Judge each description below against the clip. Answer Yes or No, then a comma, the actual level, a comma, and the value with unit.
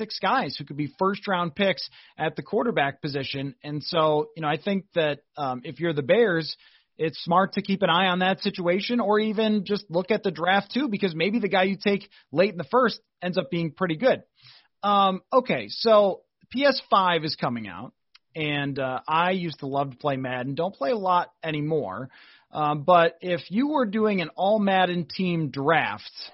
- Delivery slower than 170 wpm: No, average, 200 wpm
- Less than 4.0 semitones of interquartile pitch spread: No, average, 4.8 semitones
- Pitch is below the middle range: No, medium, 180 Hz